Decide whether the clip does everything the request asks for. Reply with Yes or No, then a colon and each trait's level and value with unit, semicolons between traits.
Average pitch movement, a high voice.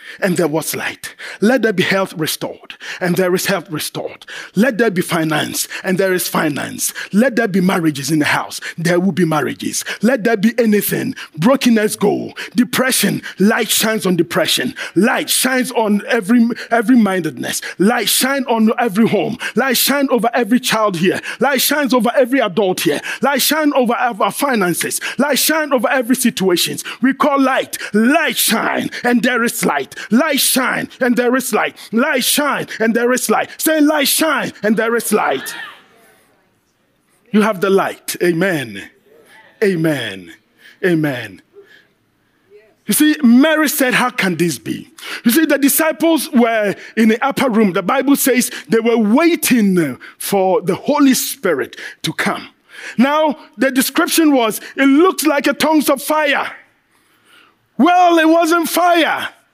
No: wide, 5.7 semitones; high, 235 Hz